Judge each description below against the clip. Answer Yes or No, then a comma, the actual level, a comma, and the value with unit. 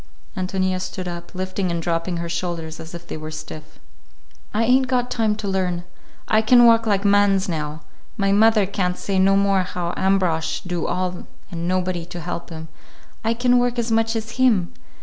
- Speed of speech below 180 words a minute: No, average, 190 wpm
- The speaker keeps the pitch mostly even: No, average, 3.9 semitones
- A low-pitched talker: No, medium, 185 Hz